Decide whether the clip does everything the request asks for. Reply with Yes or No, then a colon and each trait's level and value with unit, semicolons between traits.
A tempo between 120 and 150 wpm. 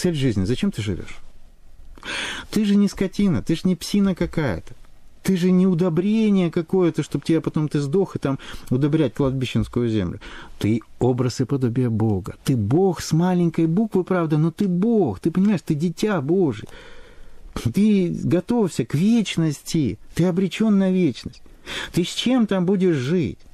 No: fast, 160 wpm